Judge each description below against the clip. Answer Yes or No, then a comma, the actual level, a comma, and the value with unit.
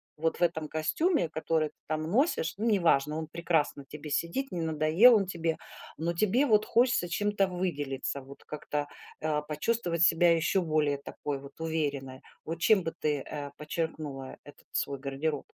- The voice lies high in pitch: No, medium, 160 Hz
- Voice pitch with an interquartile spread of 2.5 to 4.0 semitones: Yes, average, 3.1 semitones